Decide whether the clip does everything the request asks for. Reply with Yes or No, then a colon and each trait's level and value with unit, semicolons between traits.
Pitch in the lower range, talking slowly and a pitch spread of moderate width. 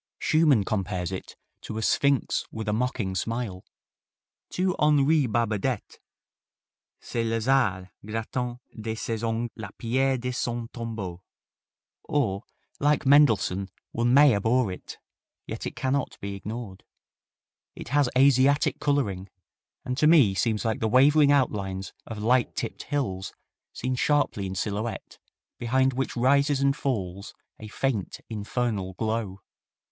Yes: low, 115 Hz; slow, 130 wpm; average, 4.6 semitones